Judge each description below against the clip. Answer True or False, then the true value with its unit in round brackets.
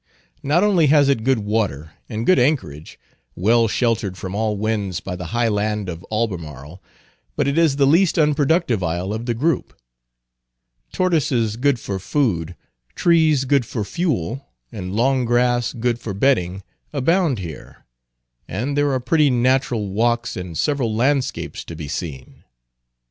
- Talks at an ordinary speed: True (150 wpm)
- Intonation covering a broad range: True (6.0 semitones)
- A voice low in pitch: True (120 Hz)